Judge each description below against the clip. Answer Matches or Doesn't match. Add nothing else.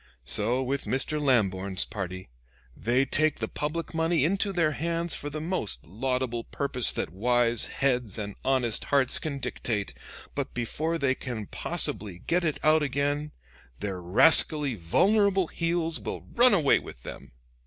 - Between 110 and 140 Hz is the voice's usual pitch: Matches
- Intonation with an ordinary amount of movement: Doesn't match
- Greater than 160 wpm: Doesn't match